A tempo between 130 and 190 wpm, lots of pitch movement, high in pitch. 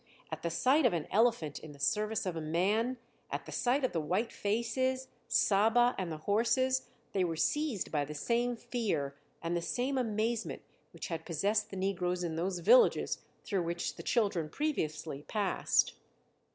Yes: average, 175 wpm; wide, 6.3 semitones; high, 205 Hz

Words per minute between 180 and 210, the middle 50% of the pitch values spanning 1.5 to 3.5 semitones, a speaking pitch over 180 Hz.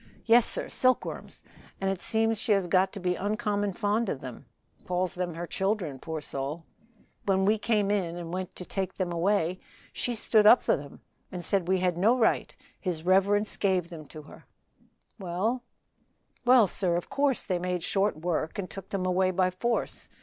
Yes: average, 185 wpm; average, 2.9 semitones; high, 190 Hz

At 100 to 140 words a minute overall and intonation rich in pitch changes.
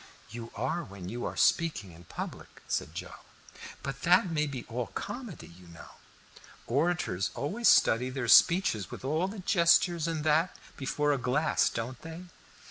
No: average, 160 wpm; wide, 6.5 semitones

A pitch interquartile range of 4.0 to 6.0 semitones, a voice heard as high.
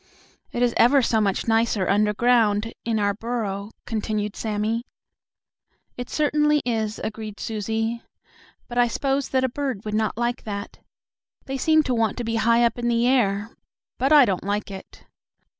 No: average, 2.7 semitones; high, 230 Hz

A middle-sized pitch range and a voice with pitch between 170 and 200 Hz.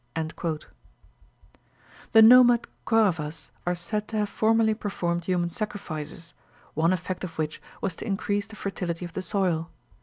Yes: average, 4.0 semitones; medium, 185 Hz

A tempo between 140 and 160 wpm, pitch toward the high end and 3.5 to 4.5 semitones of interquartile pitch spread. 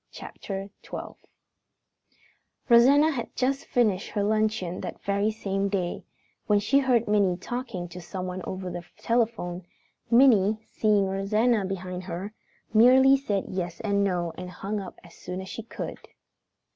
Yes: average, 145 wpm; high, 200 Hz; average, 3.8 semitones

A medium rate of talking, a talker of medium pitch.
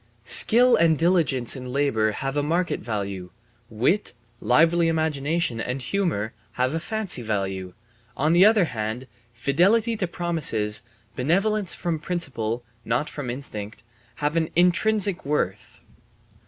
No: slow, 125 wpm; medium, 150 Hz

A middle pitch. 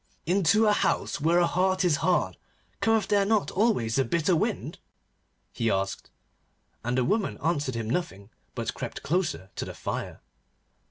Yes: medium, 175 Hz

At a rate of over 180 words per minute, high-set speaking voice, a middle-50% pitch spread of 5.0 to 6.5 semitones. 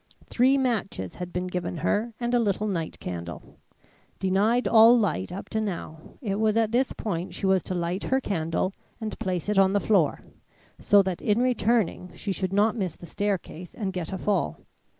No: average, 190 wpm; high, 195 Hz; average, 3.5 semitones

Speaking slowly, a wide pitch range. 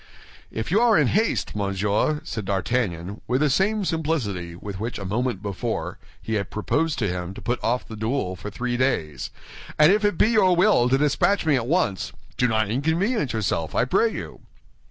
No: average, 195 wpm; wide, 8.0 semitones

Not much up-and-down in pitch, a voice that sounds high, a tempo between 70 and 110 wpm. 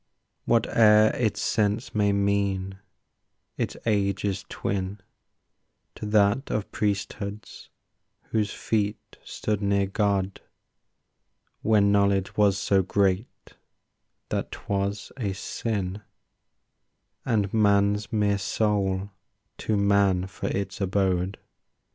No: narrow, 1.3 semitones; low, 100 Hz; slow, 100 wpm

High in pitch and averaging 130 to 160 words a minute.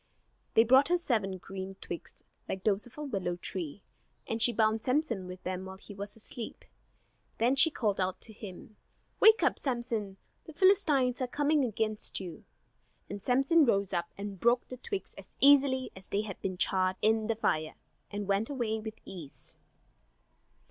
No: high, 220 Hz; average, 175 wpm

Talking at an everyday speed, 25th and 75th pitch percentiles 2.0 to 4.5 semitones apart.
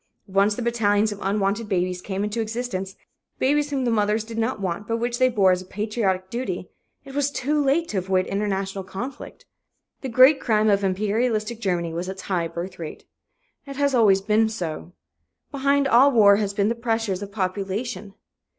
Yes: average, 185 wpm; average, 3.7 semitones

